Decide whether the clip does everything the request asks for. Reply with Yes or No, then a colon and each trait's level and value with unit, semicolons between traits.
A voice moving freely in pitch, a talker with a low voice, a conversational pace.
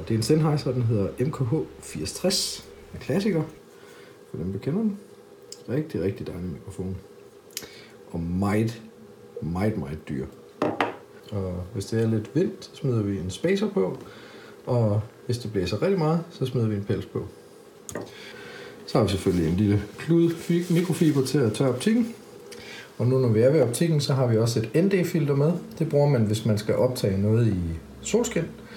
Yes: wide, 8.5 semitones; low, 125 Hz; average, 175 wpm